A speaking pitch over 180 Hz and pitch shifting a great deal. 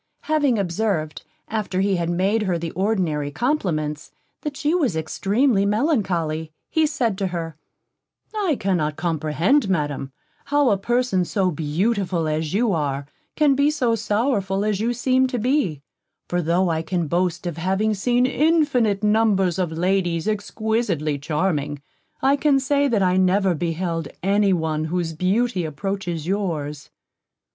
Yes: high, 190 Hz; wide, 5.9 semitones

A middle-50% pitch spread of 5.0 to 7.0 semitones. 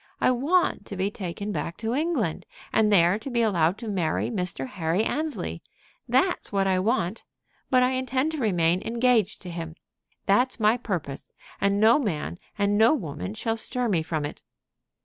Yes: wide, 5.5 semitones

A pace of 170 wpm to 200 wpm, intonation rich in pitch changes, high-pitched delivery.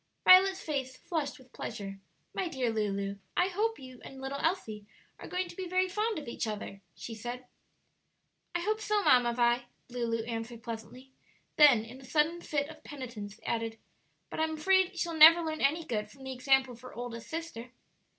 Yes: average, 185 wpm; wide, 6.1 semitones; very high, 265 Hz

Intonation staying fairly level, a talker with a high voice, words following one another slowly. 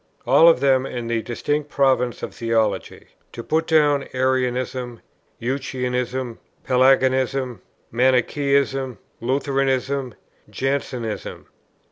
No: narrow, 1.8 semitones; low, 130 Hz; slow, 90 wpm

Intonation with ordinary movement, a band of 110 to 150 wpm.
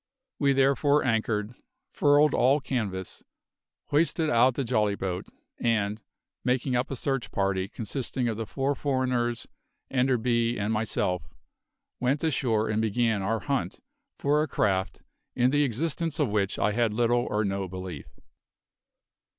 Yes: average, 4.3 semitones; average, 140 wpm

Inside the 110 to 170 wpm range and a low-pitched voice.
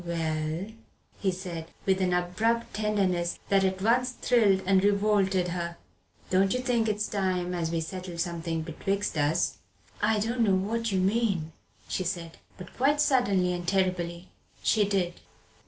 No: average, 155 wpm; high, 190 Hz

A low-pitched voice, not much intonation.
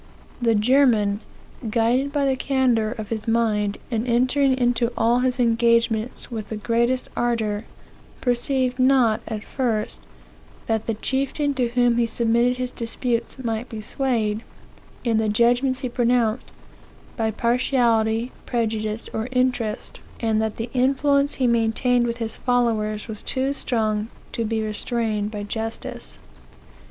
No: high, 235 Hz; narrow, 2.3 semitones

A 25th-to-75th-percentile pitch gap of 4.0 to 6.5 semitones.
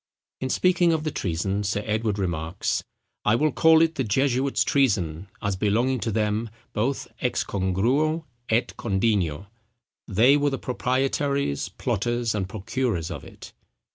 Yes: wide, 5.6 semitones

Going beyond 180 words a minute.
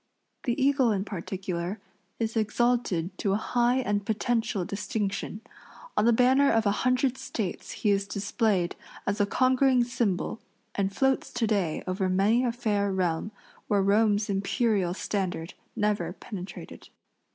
No: average, 140 wpm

